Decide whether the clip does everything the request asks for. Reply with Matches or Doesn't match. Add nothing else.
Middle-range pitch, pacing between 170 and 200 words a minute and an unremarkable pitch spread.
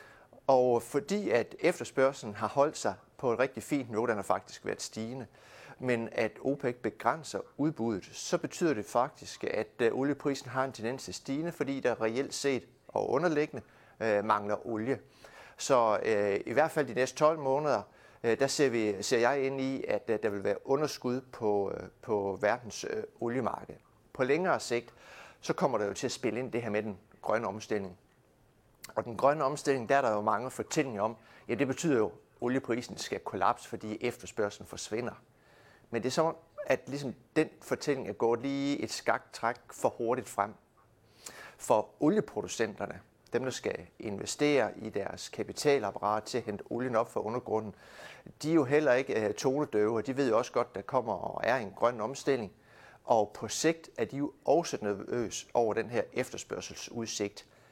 Doesn't match